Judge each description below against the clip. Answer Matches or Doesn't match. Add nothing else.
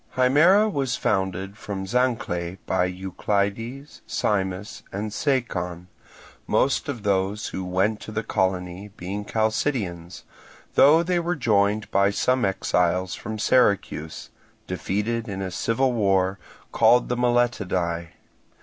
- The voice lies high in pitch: Doesn't match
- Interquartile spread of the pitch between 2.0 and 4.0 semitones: Doesn't match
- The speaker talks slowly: Matches